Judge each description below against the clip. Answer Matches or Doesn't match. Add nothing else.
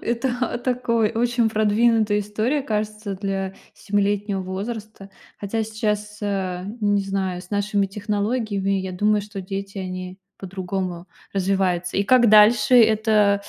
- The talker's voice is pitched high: Matches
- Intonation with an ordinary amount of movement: Doesn't match